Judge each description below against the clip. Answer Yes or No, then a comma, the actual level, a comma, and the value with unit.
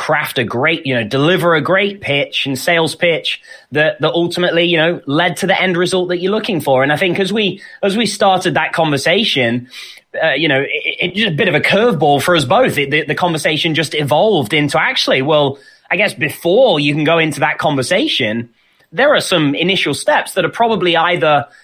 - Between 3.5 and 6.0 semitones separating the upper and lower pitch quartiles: Yes, average, 4.0 semitones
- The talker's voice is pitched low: No, medium, 160 Hz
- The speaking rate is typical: No, fast, 215 wpm